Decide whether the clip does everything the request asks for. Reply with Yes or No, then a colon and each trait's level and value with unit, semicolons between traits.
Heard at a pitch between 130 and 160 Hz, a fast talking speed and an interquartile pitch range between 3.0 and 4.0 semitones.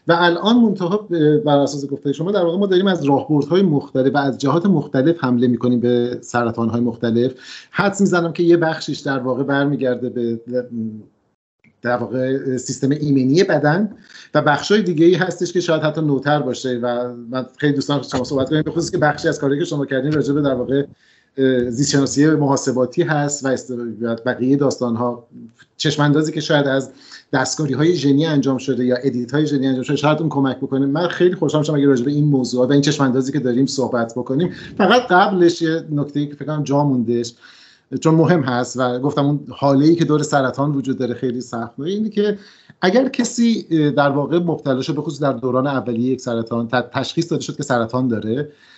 Yes: medium, 140 Hz; fast, 190 wpm; average, 3.5 semitones